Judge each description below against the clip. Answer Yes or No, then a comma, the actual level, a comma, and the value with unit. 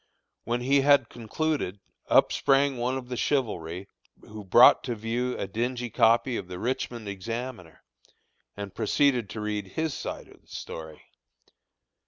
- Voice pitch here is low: Yes, low, 120 Hz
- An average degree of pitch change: Yes, average, 4.0 semitones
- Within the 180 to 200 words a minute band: No, average, 150 wpm